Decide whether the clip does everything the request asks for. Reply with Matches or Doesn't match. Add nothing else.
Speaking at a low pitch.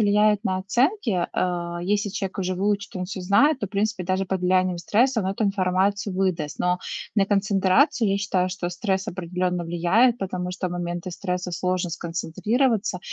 Doesn't match